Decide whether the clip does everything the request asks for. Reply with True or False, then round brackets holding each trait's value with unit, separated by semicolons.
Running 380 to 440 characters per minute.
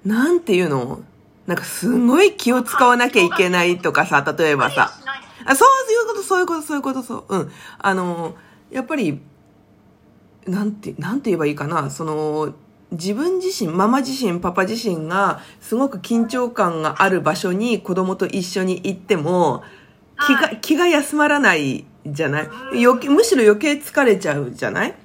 False (325 characters per minute)